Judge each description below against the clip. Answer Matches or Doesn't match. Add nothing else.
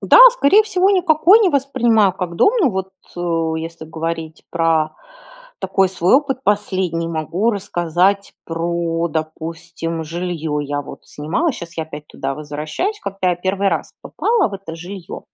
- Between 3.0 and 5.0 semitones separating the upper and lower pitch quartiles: Matches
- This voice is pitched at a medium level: Matches